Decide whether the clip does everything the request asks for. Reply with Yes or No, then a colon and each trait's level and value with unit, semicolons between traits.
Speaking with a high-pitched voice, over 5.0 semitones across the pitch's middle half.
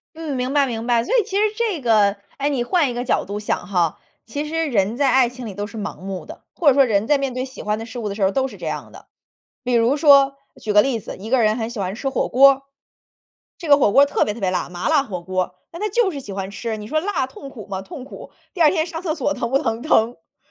Yes: high, 245 Hz; wide, 5.4 semitones